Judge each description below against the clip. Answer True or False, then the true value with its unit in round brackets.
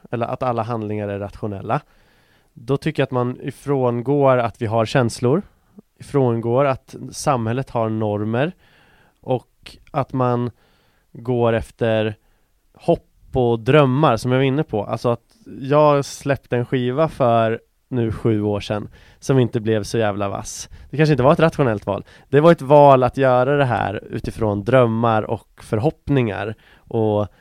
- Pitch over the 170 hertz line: False (120 Hz)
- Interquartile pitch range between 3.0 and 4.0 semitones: True (3.4 semitones)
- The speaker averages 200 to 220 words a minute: False (155 wpm)